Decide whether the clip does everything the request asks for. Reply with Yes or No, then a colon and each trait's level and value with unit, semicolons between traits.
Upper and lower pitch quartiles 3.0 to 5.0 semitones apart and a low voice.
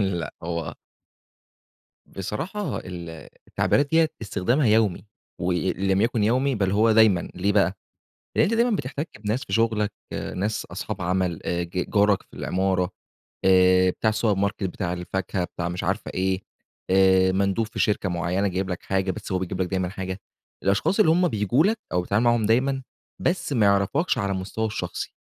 Yes: average, 3.4 semitones; low, 100 Hz